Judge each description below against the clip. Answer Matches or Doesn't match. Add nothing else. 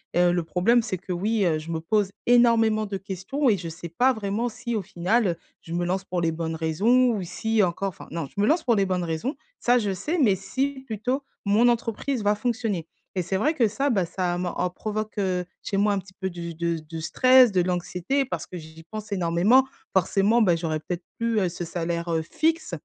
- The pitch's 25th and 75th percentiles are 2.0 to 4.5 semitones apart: Doesn't match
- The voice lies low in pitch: Doesn't match